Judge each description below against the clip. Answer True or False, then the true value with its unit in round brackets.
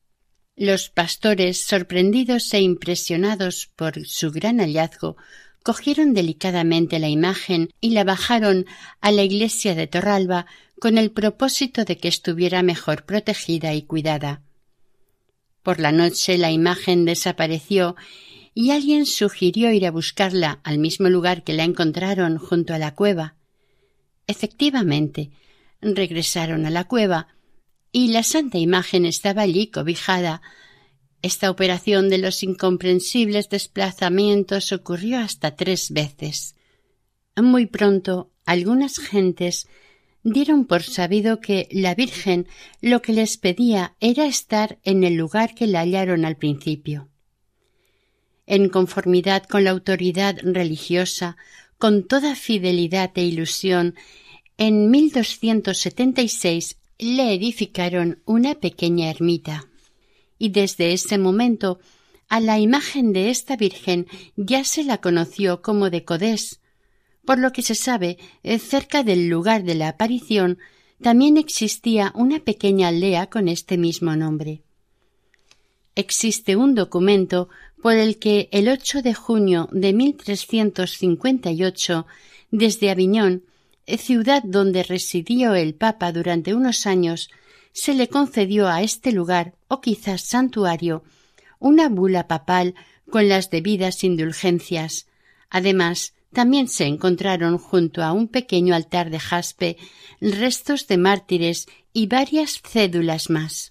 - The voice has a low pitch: False (190 Hz)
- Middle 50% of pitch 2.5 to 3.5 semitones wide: False (4.2 semitones)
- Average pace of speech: False (120 wpm)